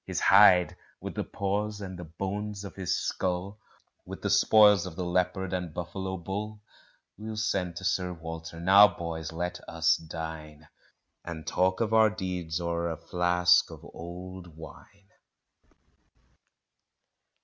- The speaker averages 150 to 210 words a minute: No, average, 140 wpm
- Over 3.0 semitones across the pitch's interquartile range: No, narrow, 2.6 semitones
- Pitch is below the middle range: Yes, very low, 90 Hz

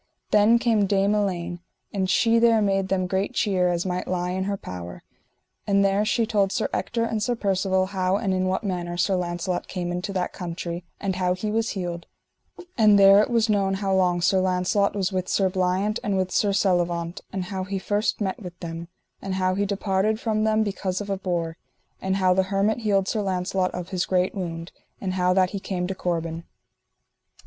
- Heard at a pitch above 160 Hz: Yes, high, 190 Hz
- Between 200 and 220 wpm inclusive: Yes, fast, 205 wpm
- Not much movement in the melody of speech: Yes, narrow, 2.0 semitones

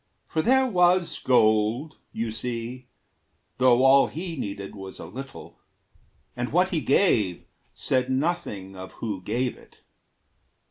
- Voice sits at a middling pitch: No, low, 125 Hz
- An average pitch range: No, wide, 6.7 semitones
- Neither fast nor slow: No, slow, 130 wpm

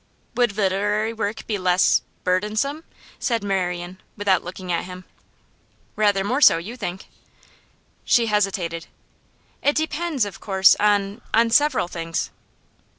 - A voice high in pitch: Yes, high, 205 Hz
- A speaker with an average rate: No, slow, 125 wpm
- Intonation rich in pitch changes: No, average, 3.7 semitones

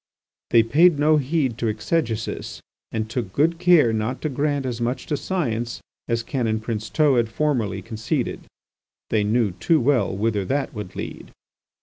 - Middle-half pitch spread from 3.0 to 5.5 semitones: Yes, average, 4.8 semitones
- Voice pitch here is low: Yes, low, 120 Hz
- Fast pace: No, average, 155 wpm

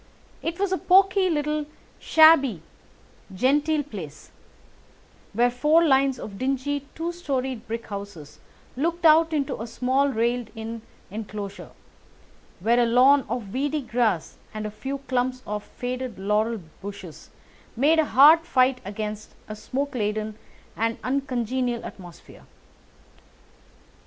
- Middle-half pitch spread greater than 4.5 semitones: Yes, average, 4.9 semitones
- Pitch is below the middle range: No, very high, 250 Hz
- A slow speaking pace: Yes, slow, 125 wpm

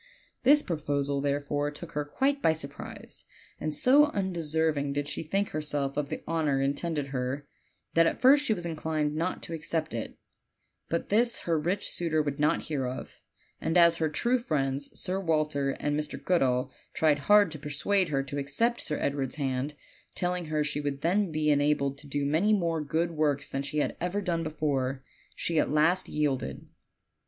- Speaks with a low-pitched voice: No, medium, 155 Hz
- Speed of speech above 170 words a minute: Yes, average, 180 wpm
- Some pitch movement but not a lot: Yes, average, 3.0 semitones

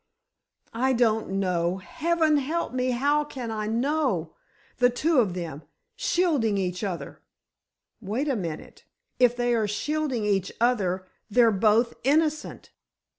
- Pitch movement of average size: No, wide, 6.2 semitones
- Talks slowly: Yes, slow, 125 wpm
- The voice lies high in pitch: Yes, high, 235 Hz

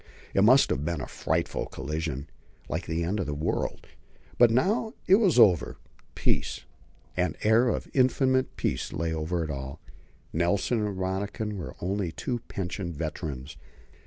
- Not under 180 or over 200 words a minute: No, average, 155 wpm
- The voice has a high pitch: No, very low, 90 Hz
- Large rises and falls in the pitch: Yes, wide, 6.2 semitones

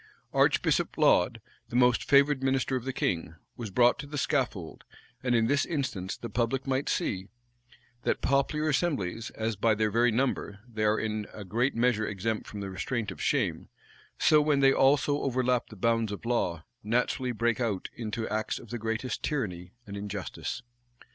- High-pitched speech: No, low, 115 Hz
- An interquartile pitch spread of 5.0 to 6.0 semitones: No, average, 3.9 semitones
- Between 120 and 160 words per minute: No, average, 175 wpm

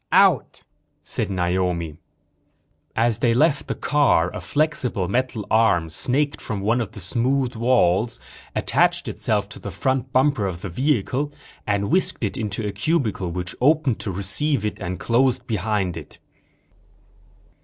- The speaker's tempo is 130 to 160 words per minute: Yes, average, 145 wpm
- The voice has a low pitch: Yes, low, 110 Hz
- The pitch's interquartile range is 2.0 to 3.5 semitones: No, average, 5.3 semitones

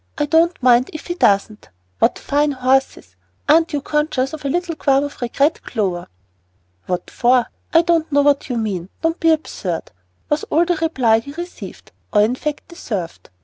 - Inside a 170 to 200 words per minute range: Yes, average, 180 wpm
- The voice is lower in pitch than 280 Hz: No, very high, 285 Hz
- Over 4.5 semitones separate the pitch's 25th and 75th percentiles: Yes, average, 5.2 semitones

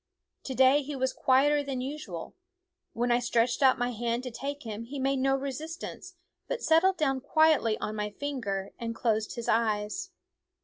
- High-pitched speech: Yes, very high, 260 Hz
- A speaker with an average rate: Yes, average, 175 wpm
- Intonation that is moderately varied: Yes, average, 3.8 semitones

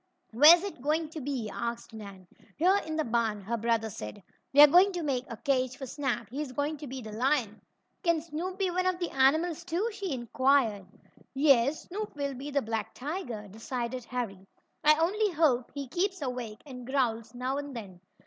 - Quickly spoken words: No, average, 190 wpm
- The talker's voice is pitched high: Yes, very high, 270 Hz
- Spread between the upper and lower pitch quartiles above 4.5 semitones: Yes, average, 5.2 semitones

